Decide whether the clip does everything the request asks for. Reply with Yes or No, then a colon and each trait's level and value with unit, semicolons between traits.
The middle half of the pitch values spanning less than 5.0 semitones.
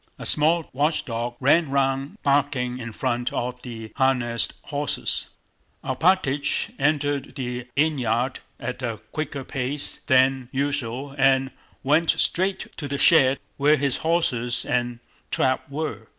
Yes: average, 2.7 semitones